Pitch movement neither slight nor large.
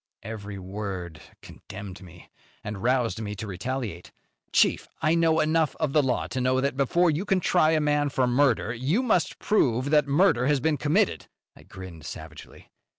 No: wide, 7.0 semitones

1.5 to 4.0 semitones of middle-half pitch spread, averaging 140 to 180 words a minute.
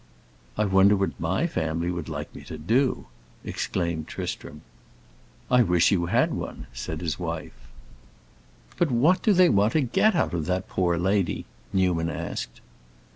No: average, 4.7 semitones; average, 155 wpm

